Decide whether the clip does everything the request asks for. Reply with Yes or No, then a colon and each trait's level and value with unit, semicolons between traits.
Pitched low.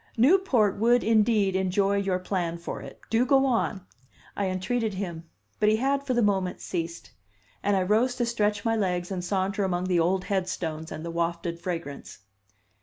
No: high, 195 Hz